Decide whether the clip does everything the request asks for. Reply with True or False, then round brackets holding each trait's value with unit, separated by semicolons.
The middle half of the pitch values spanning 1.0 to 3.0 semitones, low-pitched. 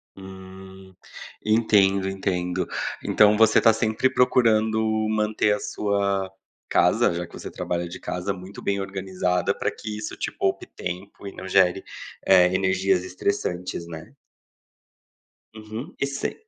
True (2.5 semitones; 95 Hz)